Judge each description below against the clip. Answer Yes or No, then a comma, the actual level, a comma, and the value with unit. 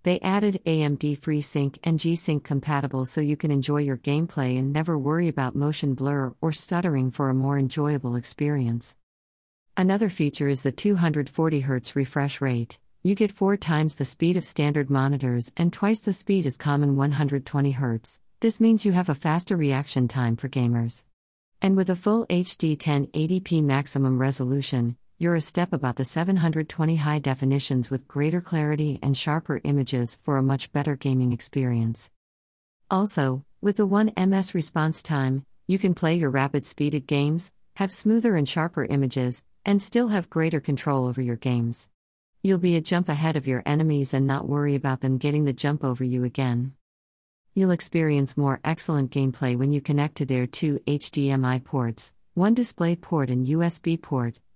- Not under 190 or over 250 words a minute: No, average, 165 wpm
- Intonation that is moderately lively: Yes, average, 3.8 semitones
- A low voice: No, medium, 145 Hz